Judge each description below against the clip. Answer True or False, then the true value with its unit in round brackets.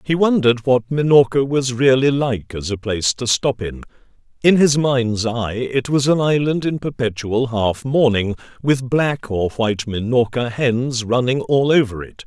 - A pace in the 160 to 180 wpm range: True (170 wpm)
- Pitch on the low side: True (125 Hz)